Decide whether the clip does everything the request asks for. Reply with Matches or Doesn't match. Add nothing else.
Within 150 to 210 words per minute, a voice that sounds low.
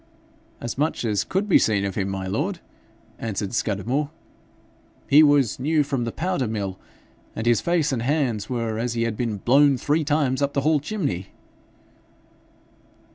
Matches